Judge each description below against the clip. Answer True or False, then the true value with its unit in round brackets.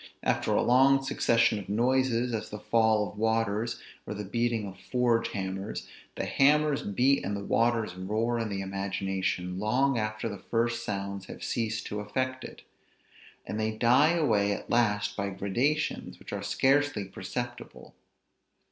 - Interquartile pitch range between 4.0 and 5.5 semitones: False (3.5 semitones)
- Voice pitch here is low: True (110 Hz)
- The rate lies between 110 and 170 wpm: True (155 wpm)